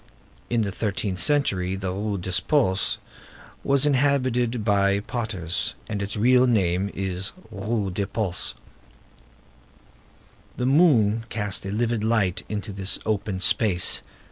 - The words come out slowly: Yes, slow, 125 wpm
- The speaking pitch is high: No, low, 105 Hz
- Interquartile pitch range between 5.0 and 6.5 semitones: No, average, 3.5 semitones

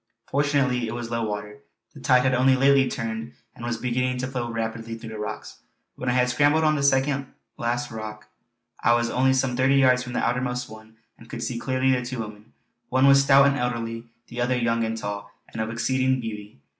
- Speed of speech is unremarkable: No, fast, 215 wpm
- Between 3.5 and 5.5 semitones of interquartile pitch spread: No, narrow, 2.4 semitones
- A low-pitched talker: Yes, low, 125 Hz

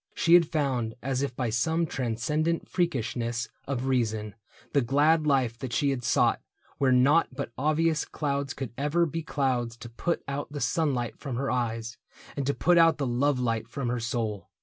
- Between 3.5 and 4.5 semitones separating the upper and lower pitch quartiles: Yes, average, 4.0 semitones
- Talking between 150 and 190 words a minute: Yes, average, 185 wpm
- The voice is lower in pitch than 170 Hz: Yes, low, 135 Hz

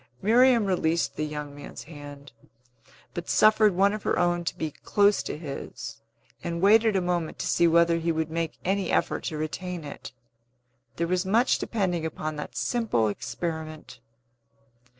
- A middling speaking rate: Yes, average, 160 wpm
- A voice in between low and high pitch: Yes, medium, 170 Hz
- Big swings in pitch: No, average, 4.0 semitones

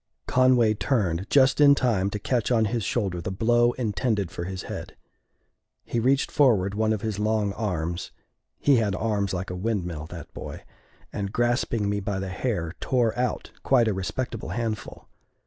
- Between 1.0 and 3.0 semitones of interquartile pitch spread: No, average, 4.0 semitones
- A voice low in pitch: Yes, low, 110 Hz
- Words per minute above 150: Yes, average, 170 wpm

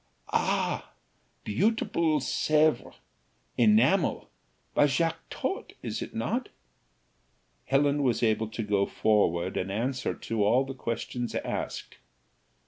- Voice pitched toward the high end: No, low, 125 Hz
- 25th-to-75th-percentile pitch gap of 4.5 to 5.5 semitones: Yes, average, 5.2 semitones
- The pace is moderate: No, slow, 105 wpm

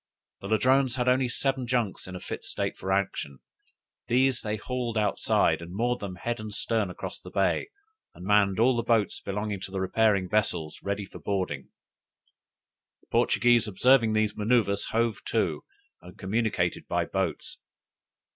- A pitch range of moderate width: Yes, average, 3.6 semitones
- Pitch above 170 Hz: No, low, 105 Hz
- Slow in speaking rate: No, average, 160 wpm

